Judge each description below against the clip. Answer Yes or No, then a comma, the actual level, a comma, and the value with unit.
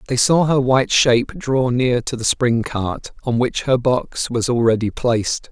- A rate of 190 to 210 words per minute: Yes, average, 195 wpm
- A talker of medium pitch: No, low, 125 Hz